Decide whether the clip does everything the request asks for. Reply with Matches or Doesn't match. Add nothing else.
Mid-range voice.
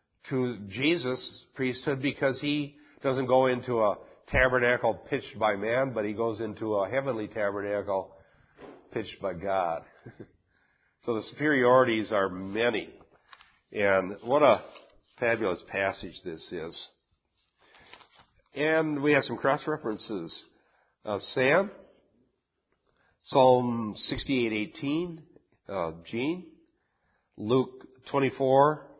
Doesn't match